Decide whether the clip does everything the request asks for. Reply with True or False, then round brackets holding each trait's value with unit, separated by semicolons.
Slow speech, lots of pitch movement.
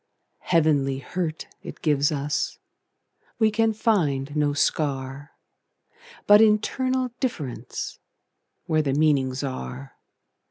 True (80 wpm; 7.3 semitones)